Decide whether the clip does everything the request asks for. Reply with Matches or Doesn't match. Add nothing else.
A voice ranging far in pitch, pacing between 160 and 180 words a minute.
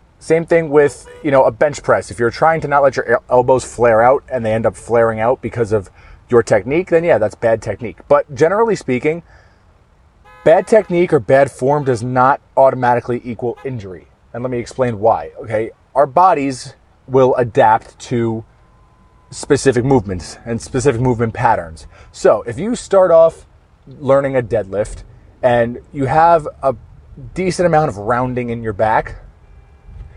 Doesn't match